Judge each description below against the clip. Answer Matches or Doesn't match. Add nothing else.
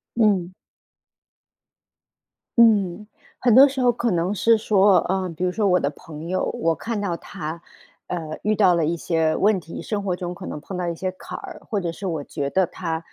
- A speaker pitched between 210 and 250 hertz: Doesn't match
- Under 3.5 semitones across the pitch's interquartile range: Doesn't match